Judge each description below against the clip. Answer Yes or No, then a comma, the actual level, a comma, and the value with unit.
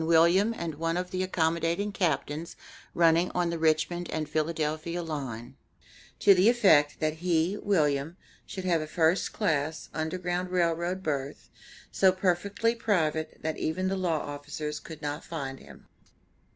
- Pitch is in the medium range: Yes, medium, 165 Hz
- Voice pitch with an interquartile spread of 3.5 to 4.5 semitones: No, average, 2.8 semitones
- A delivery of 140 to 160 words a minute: Yes, average, 150 wpm